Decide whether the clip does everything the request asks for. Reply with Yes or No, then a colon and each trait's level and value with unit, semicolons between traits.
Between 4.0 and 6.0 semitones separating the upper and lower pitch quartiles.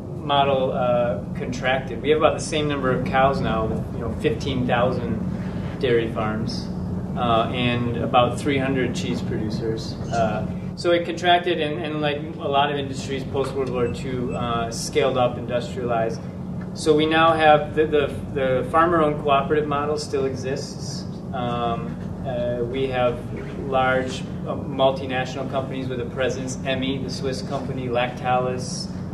No: average, 3.5 semitones